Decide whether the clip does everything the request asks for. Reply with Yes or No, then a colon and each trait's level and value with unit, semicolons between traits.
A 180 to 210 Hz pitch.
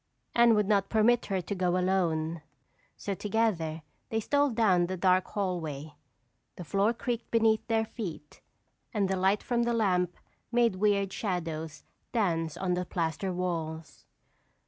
Yes: high, 190 Hz